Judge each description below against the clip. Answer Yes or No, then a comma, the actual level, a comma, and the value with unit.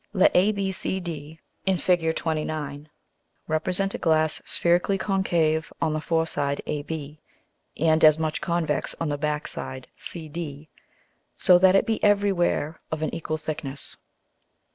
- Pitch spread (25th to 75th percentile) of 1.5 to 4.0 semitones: Yes, average, 2.8 semitones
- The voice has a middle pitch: Yes, medium, 160 Hz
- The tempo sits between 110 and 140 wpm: Yes, slow, 135 wpm